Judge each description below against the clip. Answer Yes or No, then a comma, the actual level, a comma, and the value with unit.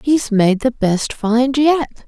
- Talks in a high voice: Yes, high, 245 Hz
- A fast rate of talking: No, average, 175 wpm